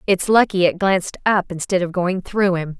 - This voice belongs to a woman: Yes, female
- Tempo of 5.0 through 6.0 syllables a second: Yes, 5.1 syllables/s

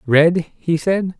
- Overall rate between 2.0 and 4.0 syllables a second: Yes, 3.0 syllables/s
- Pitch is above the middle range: No, medium, 170 Hz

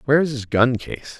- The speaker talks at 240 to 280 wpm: No, average, 200 wpm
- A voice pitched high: No, low, 125 Hz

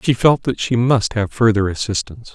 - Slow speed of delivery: No, fast, 205 wpm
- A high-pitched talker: No, low, 110 Hz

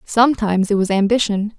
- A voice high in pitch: Yes, high, 210 Hz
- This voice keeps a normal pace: Yes, average, 150 wpm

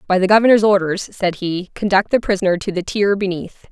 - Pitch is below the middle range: No, high, 195 Hz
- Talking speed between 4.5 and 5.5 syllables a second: No, 5.7 syllables/s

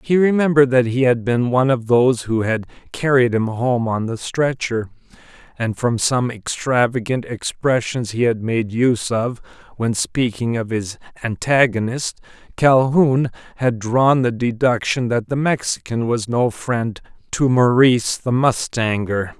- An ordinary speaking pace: Yes, average, 145 wpm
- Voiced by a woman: No, male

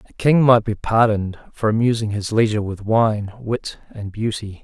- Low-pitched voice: Yes, low, 110 Hz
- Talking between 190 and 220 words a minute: No, average, 180 wpm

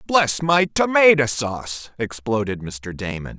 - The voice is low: Yes, low, 130 Hz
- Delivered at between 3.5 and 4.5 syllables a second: Yes, 4.2 syllables/s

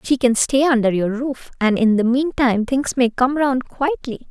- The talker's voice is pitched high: Yes, very high, 250 Hz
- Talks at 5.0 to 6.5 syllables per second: No, 4.5 syllables/s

